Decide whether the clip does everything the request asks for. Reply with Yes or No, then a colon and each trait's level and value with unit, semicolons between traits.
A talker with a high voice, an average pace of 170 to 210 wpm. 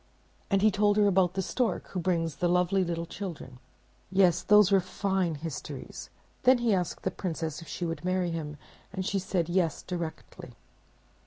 No: medium, 180 Hz; average, 175 wpm